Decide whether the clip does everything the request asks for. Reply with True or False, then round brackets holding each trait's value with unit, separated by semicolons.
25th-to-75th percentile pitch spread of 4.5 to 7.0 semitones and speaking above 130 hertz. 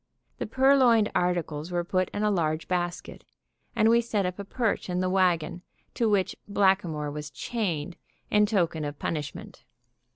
False (4.1 semitones; 185 Hz)